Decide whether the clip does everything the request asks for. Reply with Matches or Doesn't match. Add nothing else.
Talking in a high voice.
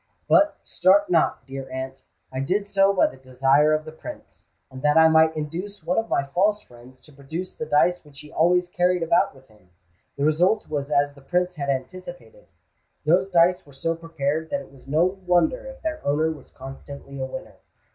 Doesn't match